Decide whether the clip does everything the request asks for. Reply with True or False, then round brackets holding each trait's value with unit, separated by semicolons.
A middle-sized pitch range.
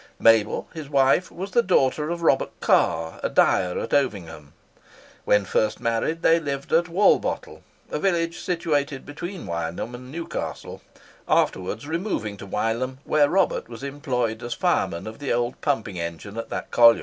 False (6.8 semitones)